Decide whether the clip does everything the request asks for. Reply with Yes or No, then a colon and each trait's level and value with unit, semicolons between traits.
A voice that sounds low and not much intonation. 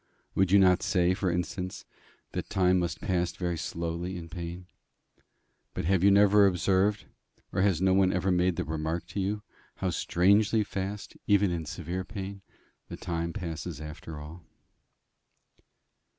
Yes: very low, 90 Hz; narrow, 2.3 semitones